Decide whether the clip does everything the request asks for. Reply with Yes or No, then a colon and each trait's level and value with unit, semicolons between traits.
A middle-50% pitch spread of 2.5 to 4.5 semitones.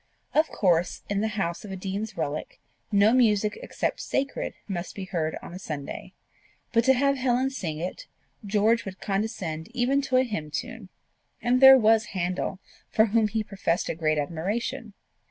No: average, 5.1 semitones